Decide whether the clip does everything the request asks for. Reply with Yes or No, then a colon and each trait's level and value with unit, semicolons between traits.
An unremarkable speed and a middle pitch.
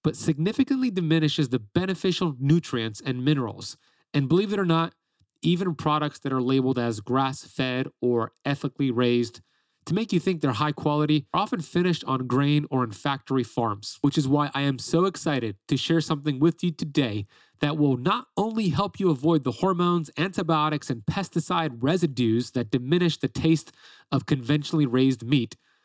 Yes: average, 170 wpm; medium, 150 Hz